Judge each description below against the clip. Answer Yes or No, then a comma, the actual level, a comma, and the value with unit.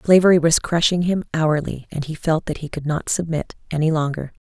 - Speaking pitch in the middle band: Yes, medium, 160 Hz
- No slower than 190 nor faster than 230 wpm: Yes, fast, 205 wpm